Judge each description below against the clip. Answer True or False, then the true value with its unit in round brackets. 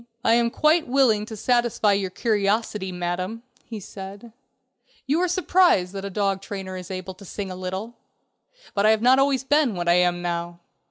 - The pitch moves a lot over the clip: False (4.3 semitones)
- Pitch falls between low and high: False (205 Hz)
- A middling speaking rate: True (185 wpm)